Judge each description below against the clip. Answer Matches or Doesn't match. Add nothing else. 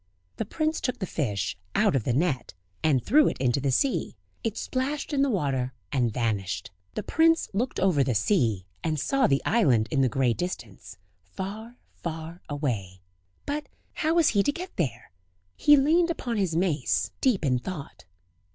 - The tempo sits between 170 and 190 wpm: Matches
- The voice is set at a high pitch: Doesn't match